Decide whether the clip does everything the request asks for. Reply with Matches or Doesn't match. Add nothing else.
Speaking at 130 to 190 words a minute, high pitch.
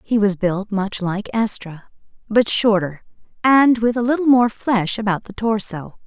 Matches